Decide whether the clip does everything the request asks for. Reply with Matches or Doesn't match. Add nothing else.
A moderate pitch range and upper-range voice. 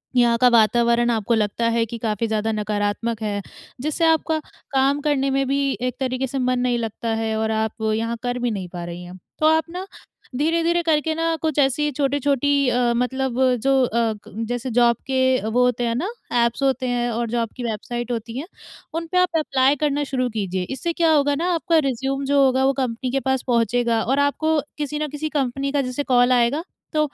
Matches